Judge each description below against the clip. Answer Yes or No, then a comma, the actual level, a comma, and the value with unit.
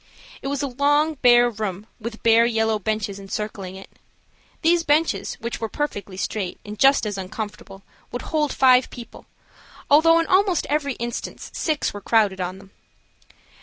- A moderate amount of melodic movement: No, wide, 5.8 semitones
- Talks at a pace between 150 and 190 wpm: Yes, average, 160 wpm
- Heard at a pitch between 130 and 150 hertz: No, high, 230 Hz